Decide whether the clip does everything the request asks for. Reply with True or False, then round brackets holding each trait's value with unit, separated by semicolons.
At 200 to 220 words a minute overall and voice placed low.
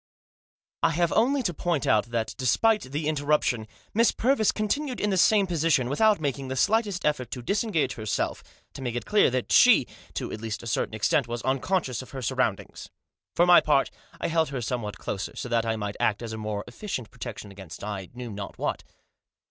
True (205 wpm; 130 Hz)